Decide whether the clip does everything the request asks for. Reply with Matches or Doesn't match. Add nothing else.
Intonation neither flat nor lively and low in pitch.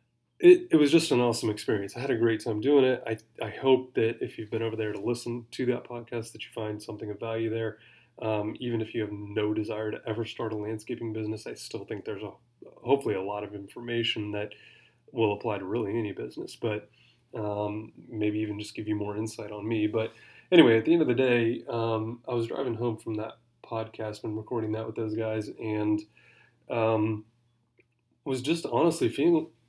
Doesn't match